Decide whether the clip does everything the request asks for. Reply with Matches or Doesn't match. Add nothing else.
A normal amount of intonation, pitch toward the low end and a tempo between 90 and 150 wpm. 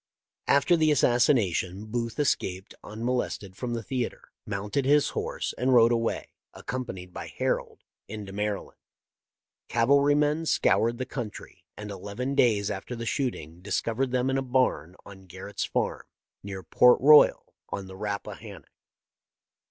Matches